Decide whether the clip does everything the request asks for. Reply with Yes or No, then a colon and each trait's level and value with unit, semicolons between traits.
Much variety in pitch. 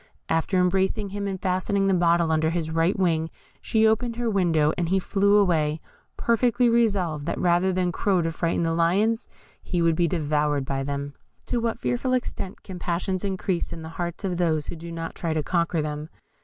No: average, 3.4 semitones